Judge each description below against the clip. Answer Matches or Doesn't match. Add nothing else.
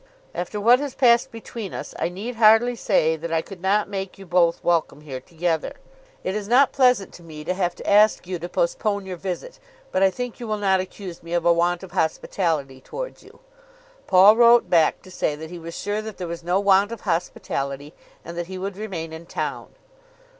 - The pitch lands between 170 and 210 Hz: Matches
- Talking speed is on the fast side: Matches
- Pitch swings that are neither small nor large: Matches